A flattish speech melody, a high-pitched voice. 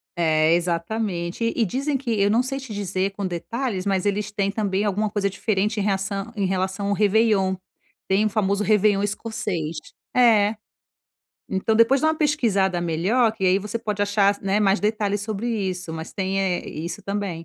Yes: narrow, 2.3 semitones; high, 200 Hz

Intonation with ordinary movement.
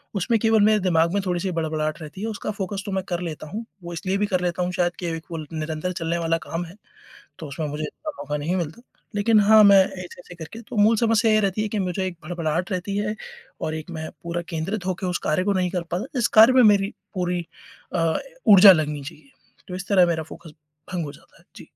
Yes: average, 3.7 semitones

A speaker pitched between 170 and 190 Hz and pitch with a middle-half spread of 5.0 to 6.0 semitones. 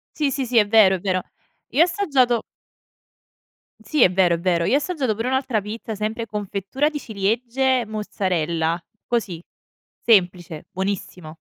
No: high, 215 Hz; wide, 5.5 semitones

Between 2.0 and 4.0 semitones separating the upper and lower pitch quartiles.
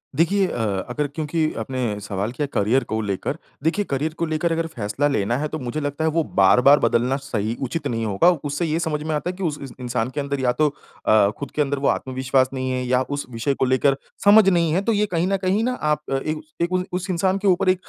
No: average, 4.9 semitones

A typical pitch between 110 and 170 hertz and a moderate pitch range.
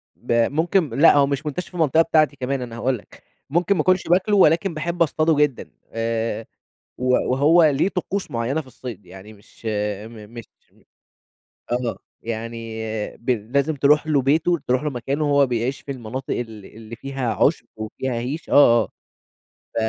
Yes: low, 135 Hz; average, 5.0 semitones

